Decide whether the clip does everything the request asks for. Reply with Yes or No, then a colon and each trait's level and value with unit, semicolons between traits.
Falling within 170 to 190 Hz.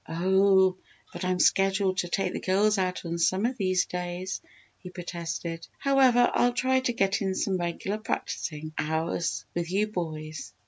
Yes: medium, 185 Hz